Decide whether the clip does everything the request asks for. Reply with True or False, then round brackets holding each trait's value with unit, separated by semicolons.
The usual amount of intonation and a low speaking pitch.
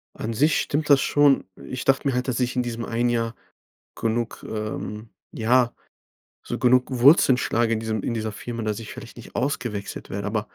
False (2.3 semitones; 120 Hz)